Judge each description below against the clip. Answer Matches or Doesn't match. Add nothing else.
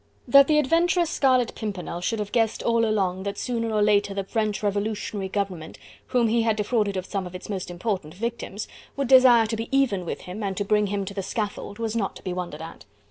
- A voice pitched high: Matches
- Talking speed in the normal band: Doesn't match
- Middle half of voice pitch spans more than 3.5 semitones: Doesn't match